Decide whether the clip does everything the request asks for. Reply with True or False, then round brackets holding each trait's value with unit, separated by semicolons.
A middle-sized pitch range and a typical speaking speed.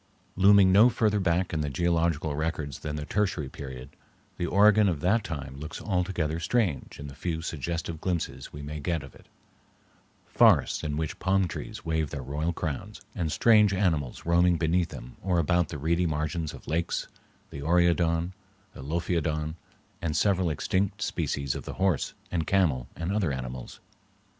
True (3.5 semitones; 165 wpm)